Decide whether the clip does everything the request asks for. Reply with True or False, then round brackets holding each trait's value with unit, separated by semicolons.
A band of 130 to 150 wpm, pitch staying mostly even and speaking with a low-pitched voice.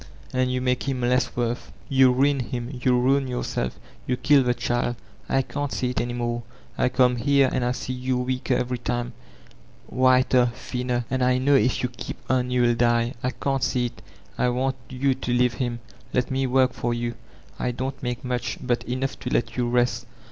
False (200 wpm; 1.1 semitones; 125 Hz)